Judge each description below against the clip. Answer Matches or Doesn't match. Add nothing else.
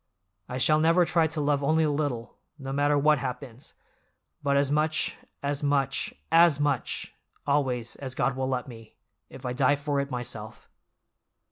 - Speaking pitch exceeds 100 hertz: Matches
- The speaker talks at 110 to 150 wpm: Doesn't match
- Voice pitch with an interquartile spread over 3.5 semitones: Doesn't match